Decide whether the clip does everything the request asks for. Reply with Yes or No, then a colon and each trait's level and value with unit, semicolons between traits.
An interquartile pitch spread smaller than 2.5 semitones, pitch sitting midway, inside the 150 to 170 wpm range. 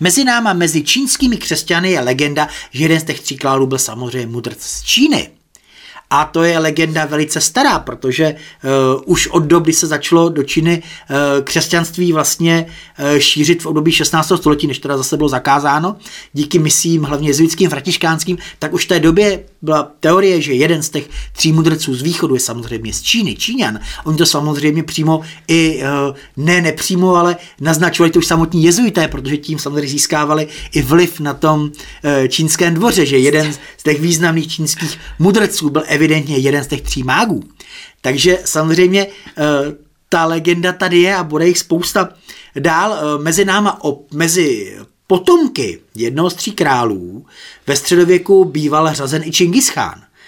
No: average, 2.9 semitones; medium, 160 Hz; average, 165 wpm